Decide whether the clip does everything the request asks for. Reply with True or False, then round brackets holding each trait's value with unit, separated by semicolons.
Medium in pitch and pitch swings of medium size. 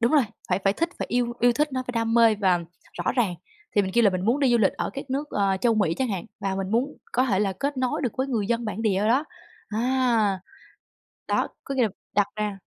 False (230 Hz; 4.3 semitones)